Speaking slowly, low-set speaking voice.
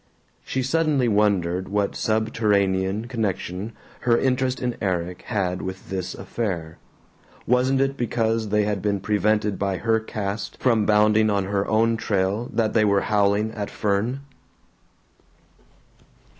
Yes: slow, 130 wpm; low, 105 Hz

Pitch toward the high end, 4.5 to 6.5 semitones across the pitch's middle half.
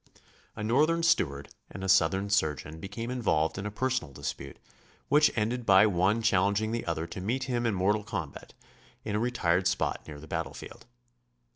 No: low, 100 Hz; wide, 5.5 semitones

